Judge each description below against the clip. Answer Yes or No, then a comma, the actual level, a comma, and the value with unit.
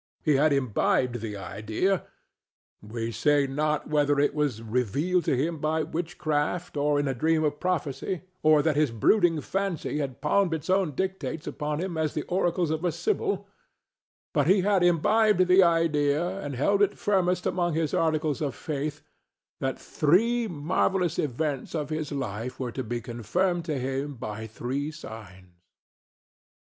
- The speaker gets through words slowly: No, average, 155 wpm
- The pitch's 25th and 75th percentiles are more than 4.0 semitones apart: Yes, average, 4.5 semitones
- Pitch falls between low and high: Yes, medium, 150 Hz